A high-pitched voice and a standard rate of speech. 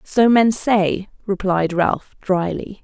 No: high, 195 Hz; slow, 125 wpm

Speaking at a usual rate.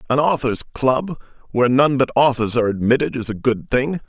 Yes: average, 190 wpm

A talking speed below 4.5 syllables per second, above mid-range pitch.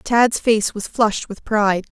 Yes: 4.3 syllables/s; high, 215 Hz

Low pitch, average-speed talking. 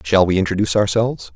Yes: low, 100 Hz; average, 180 wpm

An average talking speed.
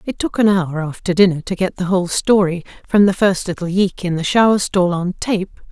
No: fast, 230 wpm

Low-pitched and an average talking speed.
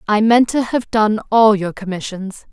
No: high, 215 Hz; average, 190 wpm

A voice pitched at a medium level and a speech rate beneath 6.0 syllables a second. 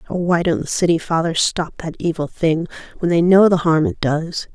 Yes: medium, 170 Hz; 5.0 syllables/s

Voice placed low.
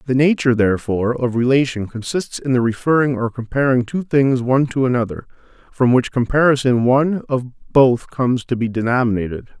Yes: low, 125 Hz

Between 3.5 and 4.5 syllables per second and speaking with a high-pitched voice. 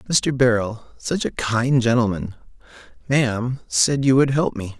No: 4.1 syllables/s; low, 120 Hz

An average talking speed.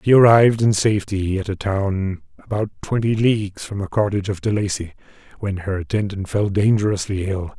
Yes: average, 175 wpm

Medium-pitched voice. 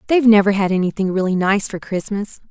No: high, 200 Hz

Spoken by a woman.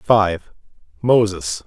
No: male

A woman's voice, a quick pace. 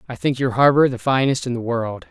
No: male; fast, 255 wpm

